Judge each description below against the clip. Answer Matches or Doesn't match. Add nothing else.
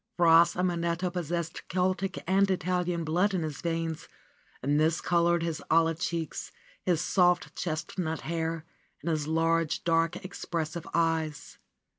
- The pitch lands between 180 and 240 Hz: Doesn't match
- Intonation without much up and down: Matches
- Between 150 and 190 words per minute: Doesn't match